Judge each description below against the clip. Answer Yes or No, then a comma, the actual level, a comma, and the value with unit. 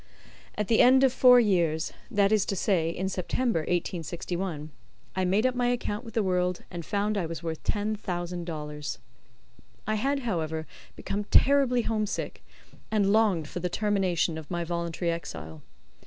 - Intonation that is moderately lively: Yes, average, 4.4 semitones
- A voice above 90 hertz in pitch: Yes, medium, 185 Hz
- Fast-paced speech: No, average, 165 wpm